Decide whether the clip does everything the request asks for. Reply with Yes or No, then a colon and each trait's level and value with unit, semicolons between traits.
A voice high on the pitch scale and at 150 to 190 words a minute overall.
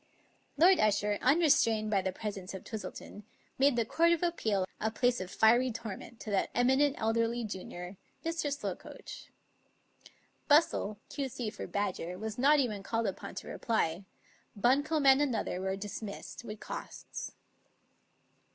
No: high, 225 Hz; average, 140 wpm